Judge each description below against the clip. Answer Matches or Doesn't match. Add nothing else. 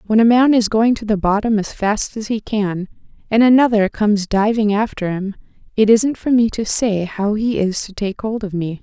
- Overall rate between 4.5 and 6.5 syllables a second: Matches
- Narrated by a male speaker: Doesn't match